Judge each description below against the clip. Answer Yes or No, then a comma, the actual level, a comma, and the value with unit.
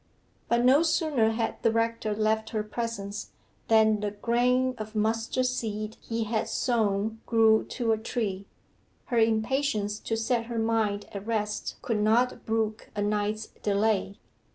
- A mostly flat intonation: Yes, narrow, 1.6 semitones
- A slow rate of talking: No, average, 150 wpm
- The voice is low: No, high, 220 Hz